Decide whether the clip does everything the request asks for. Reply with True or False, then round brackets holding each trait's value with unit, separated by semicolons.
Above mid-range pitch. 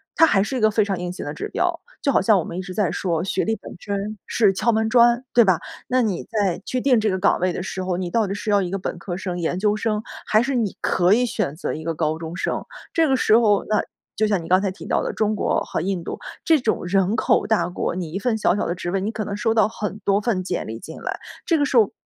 True (200 Hz)